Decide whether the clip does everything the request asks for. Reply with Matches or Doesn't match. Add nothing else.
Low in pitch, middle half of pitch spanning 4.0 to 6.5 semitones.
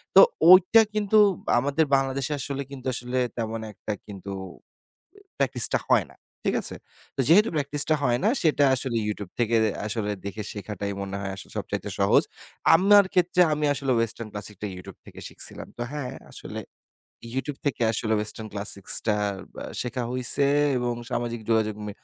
Matches